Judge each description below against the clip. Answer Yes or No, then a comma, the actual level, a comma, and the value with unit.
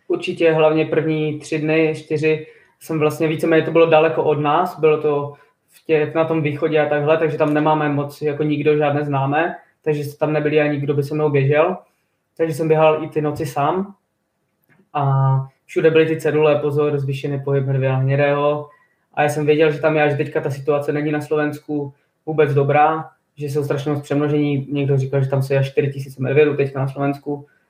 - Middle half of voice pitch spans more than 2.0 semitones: No, narrow, 1.4 semitones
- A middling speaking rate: No, fast, 195 wpm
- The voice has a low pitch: No, medium, 150 Hz